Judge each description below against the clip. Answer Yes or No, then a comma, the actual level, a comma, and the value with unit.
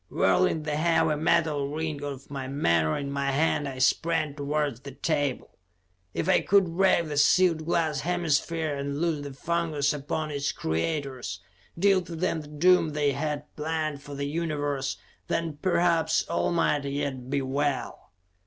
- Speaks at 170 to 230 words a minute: No, average, 160 wpm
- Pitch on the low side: No, medium, 150 Hz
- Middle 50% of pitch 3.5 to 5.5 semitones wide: No, average, 2.7 semitones